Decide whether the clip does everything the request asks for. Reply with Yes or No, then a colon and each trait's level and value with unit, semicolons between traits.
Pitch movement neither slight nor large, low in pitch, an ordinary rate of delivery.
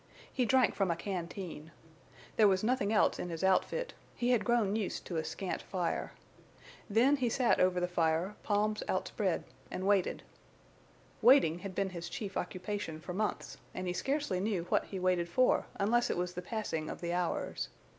No: average, 3.5 semitones; high, 190 Hz; average, 180 wpm